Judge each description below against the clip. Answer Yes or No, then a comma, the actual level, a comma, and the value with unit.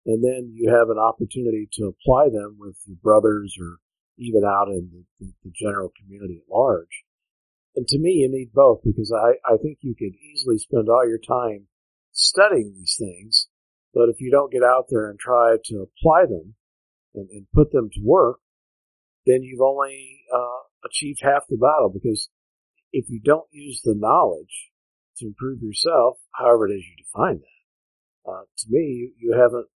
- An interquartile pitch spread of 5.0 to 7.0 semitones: No, average, 4.0 semitones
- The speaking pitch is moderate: No, low, 115 Hz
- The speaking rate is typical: Yes, average, 185 wpm